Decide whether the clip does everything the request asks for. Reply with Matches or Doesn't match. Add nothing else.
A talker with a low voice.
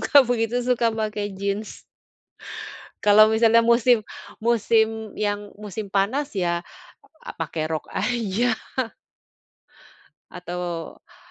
Doesn't match